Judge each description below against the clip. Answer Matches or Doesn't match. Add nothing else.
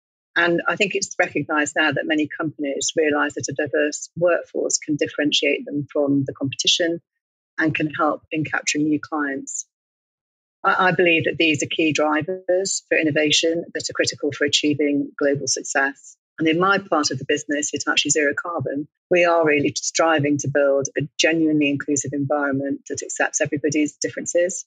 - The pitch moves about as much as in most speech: Doesn't match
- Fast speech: Doesn't match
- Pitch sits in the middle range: Matches